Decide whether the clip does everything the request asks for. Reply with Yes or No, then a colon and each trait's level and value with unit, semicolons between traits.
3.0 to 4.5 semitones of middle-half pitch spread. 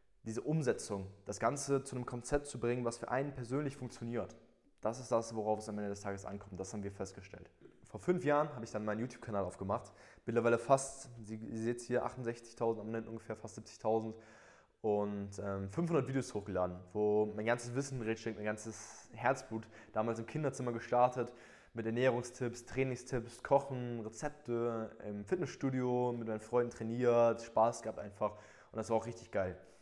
No: narrow, 2.5 semitones